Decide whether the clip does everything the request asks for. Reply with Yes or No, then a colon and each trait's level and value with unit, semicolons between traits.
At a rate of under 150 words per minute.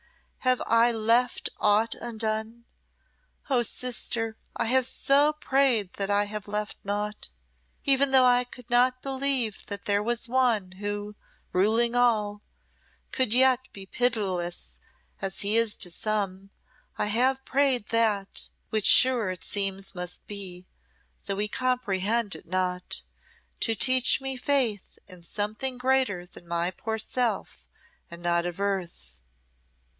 Yes: slow, 135 wpm